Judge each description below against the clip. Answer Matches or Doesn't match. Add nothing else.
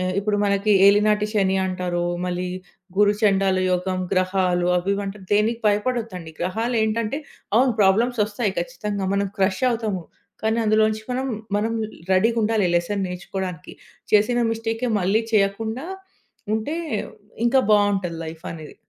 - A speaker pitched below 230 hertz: Matches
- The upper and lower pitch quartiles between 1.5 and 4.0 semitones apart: Matches